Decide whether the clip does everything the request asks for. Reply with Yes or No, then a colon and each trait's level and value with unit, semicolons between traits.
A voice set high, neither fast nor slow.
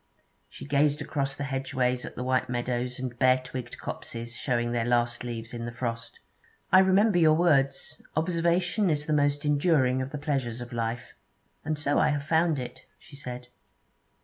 No: low, 135 Hz; average, 175 wpm